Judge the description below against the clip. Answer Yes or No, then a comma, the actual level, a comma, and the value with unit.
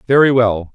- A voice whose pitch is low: Yes, low, 120 Hz